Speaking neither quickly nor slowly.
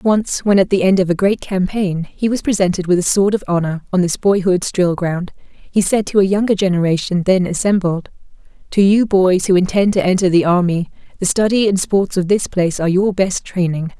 No: fast, 215 wpm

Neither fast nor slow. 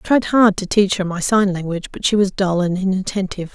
No: fast, 255 wpm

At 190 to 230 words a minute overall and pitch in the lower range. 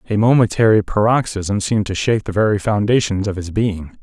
No: average, 180 wpm; low, 105 Hz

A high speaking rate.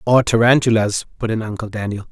No: average, 170 wpm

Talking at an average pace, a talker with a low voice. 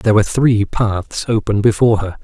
Yes: average, 190 wpm; low, 105 Hz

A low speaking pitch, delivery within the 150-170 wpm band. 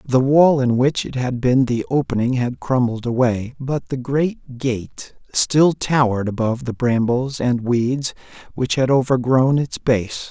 Yes: low, 125 Hz; average, 165 wpm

